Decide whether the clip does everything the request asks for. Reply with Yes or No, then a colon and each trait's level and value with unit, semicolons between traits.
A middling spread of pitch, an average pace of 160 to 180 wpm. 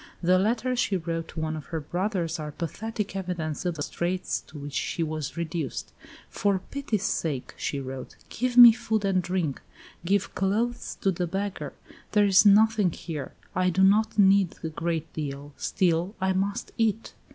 Yes: average, 4.1 semitones; average, 175 wpm